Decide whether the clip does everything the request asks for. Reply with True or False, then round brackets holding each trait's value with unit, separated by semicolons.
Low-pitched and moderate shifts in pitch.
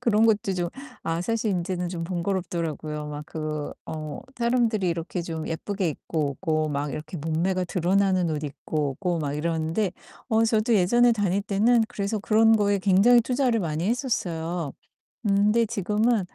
False (185 Hz; 5.0 semitones)